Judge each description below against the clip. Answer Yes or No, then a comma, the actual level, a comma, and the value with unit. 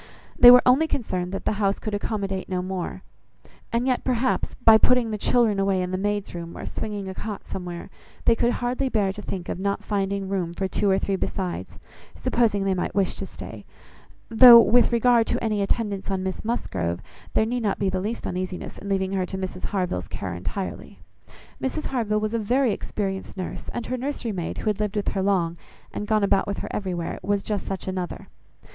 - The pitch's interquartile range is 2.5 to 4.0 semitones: Yes, average, 3.1 semitones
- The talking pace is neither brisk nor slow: No, fast, 210 wpm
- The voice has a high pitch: Yes, high, 200 Hz